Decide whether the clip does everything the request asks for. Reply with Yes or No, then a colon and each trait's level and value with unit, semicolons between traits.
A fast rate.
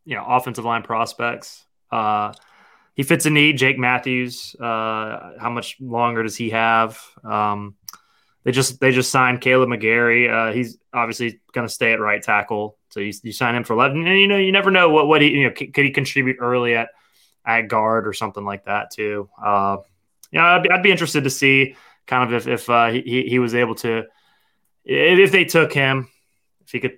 Yes: fast, 210 wpm